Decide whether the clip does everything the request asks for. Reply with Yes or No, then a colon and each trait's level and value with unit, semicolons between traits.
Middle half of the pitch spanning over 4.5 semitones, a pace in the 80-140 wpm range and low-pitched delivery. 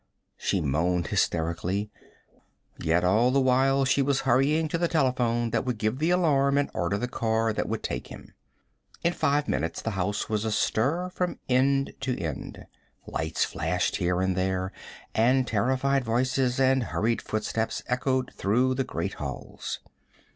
No: average, 5.3 semitones; average, 155 wpm; low, 120 Hz